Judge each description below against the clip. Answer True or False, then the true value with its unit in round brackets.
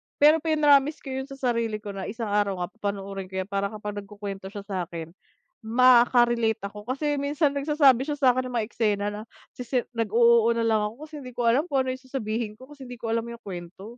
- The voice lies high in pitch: True (235 Hz)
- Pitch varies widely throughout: False (4.1 semitones)